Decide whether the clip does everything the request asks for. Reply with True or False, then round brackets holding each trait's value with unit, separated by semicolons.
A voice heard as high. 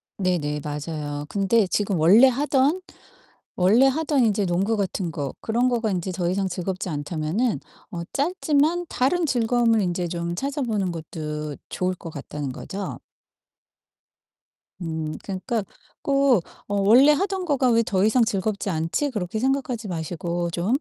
True (200 Hz)